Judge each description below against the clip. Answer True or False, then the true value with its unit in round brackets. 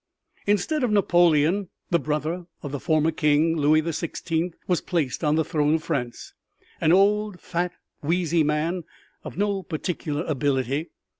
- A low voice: False (165 Hz)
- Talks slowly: False (150 wpm)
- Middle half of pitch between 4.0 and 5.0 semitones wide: False (2.9 semitones)